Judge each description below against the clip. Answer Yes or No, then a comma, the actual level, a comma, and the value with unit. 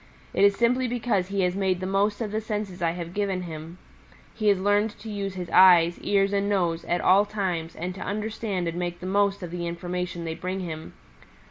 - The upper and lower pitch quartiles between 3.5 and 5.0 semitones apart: No, narrow, 2.6 semitones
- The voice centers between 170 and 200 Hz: Yes, high, 190 Hz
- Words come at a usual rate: No, fast, 220 wpm